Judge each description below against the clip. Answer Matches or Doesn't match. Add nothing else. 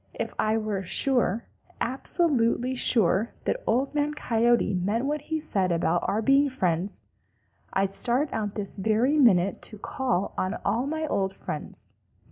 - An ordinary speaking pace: Matches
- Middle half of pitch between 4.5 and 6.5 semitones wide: Matches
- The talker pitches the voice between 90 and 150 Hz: Doesn't match